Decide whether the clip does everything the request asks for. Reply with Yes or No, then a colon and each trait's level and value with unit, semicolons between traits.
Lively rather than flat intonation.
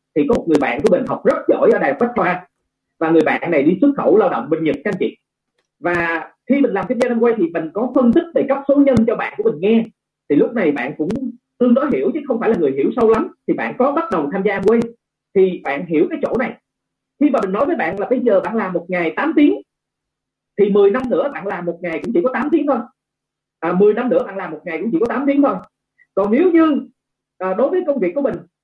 Yes: wide, 7.2 semitones